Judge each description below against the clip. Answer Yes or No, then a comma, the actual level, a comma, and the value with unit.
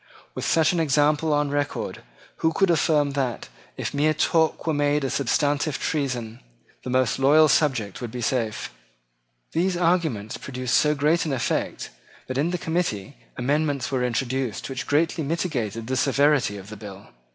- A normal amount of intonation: Yes, average, 3.8 semitones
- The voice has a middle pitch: Yes, medium, 145 Hz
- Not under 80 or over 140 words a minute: No, average, 165 wpm